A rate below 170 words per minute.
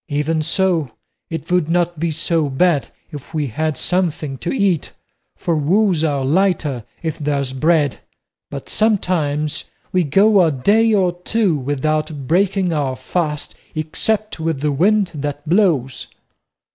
Yes: average, 140 wpm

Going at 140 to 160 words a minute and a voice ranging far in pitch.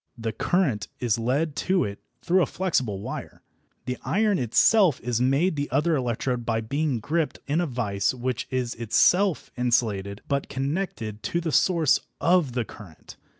Yes: average, 155 wpm; wide, 6.4 semitones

